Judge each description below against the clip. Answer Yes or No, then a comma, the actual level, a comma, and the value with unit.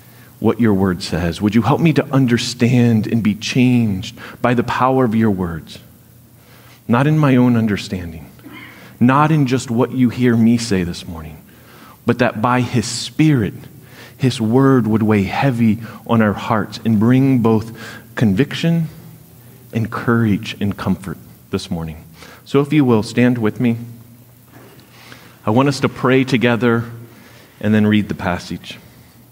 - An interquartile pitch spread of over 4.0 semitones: No, narrow, 2.6 semitones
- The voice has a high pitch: No, low, 120 Hz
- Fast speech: No, average, 155 wpm